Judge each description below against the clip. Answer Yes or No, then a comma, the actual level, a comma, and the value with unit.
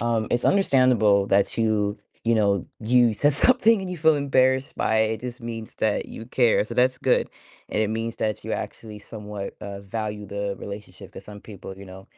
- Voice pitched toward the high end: No, low, 110 Hz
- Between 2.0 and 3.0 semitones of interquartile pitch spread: No, average, 3.5 semitones